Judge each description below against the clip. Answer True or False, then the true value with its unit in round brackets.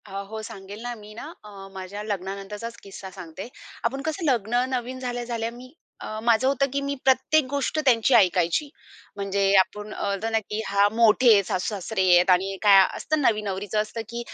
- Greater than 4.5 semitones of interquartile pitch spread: False (3.6 semitones)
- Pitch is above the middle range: True (215 Hz)